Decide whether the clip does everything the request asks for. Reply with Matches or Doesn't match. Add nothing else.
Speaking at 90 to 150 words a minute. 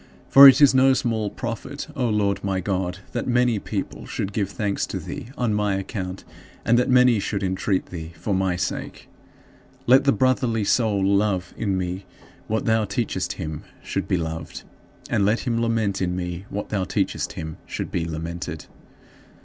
Doesn't match